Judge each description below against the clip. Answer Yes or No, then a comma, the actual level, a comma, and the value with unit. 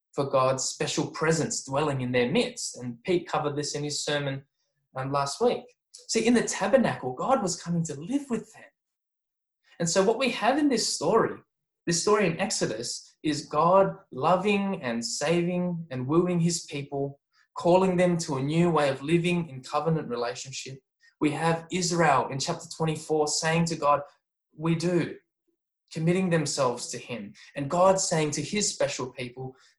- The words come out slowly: No, average, 165 wpm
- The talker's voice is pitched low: No, medium, 165 Hz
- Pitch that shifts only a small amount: No, average, 4.7 semitones